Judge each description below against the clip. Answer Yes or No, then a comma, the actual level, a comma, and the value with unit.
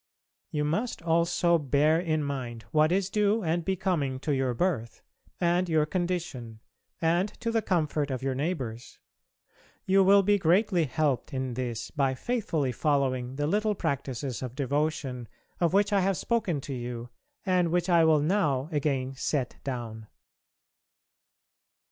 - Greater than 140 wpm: Yes, average, 150 wpm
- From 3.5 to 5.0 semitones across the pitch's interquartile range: No, wide, 5.4 semitones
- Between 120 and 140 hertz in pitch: No, medium, 155 Hz